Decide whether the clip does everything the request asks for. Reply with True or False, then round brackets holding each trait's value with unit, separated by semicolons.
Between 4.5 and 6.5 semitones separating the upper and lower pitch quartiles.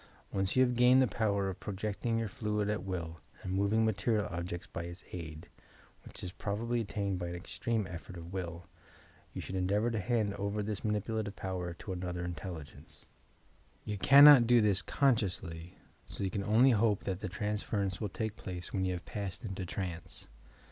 False (3.3 semitones)